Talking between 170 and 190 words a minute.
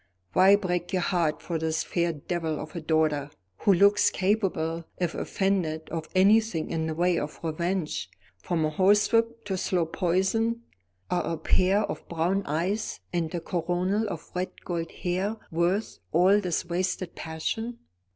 No: average, 155 wpm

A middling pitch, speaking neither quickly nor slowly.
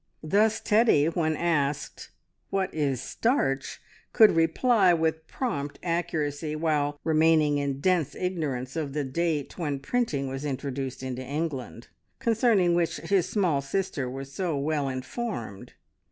No: medium, 155 Hz; slow, 130 wpm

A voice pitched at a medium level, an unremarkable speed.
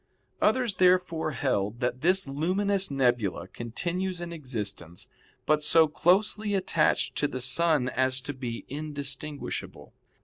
No: medium, 150 Hz; slow, 125 wpm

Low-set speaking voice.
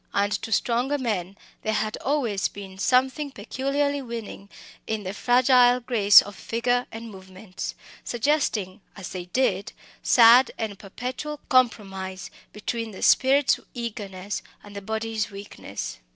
No: high, 225 Hz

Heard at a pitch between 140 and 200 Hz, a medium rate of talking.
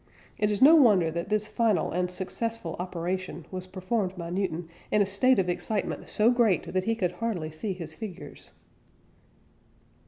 Yes: high, 190 Hz; average, 165 wpm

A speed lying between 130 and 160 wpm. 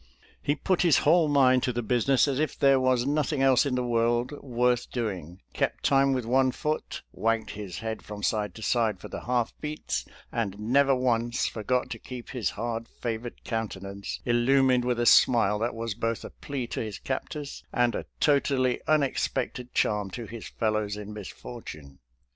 No: average, 180 wpm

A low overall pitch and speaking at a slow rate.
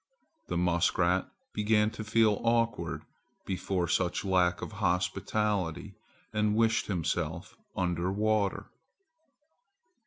Yes: very low, 95 Hz; slow, 95 wpm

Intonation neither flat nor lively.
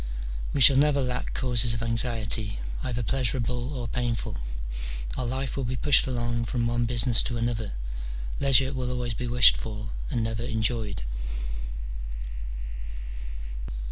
No: narrow, 1.8 semitones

